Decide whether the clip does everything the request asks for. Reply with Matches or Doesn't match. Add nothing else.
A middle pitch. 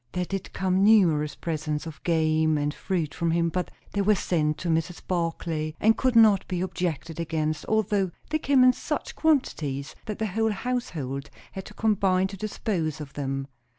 Matches